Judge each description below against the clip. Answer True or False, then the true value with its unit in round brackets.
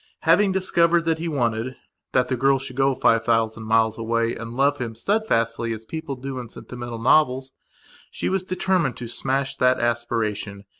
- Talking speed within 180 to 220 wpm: False (165 wpm)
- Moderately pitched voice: False (125 Hz)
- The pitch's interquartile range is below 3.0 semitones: False (3.8 semitones)